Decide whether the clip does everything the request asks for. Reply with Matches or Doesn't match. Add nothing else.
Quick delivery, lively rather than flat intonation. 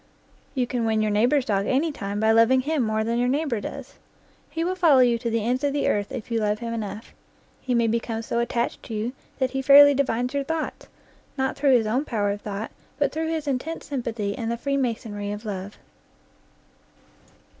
Doesn't match